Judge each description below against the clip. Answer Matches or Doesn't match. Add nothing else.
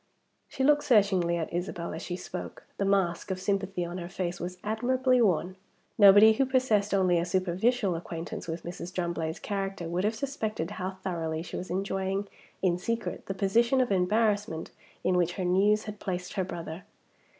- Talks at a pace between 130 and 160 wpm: Doesn't match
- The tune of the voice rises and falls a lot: Doesn't match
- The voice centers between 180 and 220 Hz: Matches